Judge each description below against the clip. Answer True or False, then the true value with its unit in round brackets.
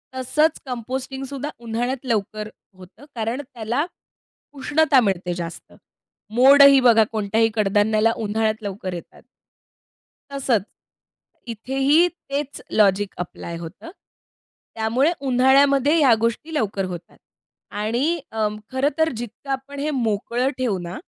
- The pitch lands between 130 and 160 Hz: False (235 Hz)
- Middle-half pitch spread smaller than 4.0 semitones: False (4.4 semitones)